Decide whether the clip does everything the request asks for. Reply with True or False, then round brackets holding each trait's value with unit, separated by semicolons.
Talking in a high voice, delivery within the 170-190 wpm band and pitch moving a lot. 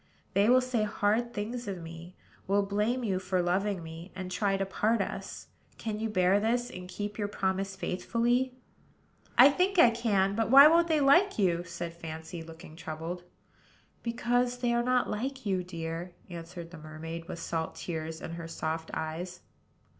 True (195 Hz; 175 wpm; 5.7 semitones)